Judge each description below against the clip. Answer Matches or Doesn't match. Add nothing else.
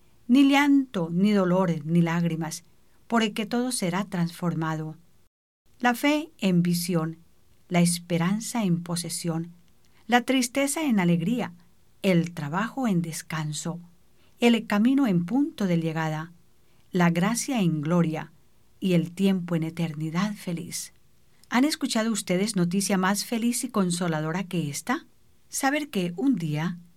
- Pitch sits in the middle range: Matches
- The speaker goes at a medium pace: Doesn't match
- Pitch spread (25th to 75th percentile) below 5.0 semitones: Doesn't match